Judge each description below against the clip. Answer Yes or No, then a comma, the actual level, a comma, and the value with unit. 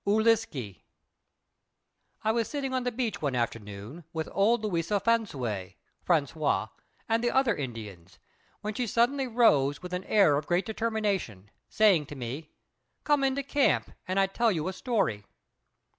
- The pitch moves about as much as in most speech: No, wide, 8.5 semitones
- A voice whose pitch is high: Yes, high, 195 Hz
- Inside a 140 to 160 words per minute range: Yes, average, 150 wpm